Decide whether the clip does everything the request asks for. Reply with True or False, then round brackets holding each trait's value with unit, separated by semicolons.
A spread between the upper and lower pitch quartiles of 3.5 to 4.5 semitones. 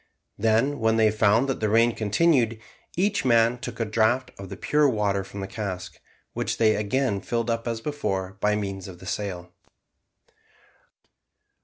False (3.0 semitones)